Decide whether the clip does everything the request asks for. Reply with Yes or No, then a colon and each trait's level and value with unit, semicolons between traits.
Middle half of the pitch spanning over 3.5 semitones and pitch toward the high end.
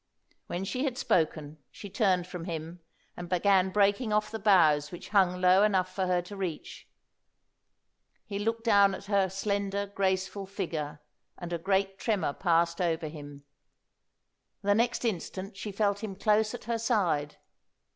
No: average, 2.8 semitones; high, 195 Hz